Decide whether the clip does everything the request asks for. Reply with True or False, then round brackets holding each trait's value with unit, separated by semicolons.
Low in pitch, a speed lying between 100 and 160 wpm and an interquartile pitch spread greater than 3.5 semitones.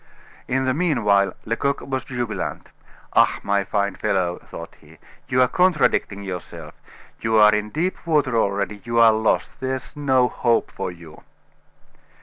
True (115 Hz; 150 wpm; 4.7 semitones)